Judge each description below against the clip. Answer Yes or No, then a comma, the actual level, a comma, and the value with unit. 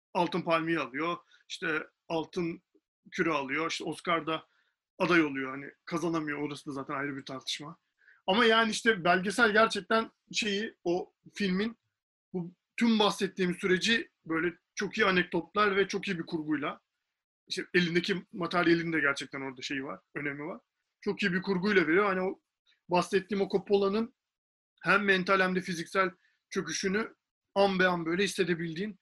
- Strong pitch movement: No, average, 3.2 semitones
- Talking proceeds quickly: Yes, fast, 145 wpm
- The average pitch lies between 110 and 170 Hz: No, medium, 185 Hz